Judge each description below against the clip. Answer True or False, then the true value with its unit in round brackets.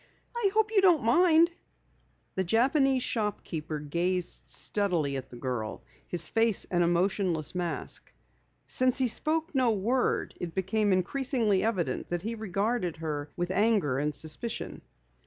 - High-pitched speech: True (195 Hz)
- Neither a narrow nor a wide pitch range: False (6.4 semitones)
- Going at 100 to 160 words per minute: True (140 wpm)